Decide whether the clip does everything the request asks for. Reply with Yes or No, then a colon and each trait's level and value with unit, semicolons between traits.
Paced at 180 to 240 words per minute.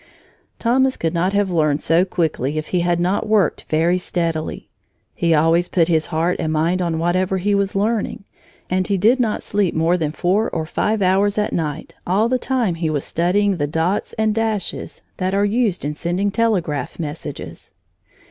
Yes: average, 185 wpm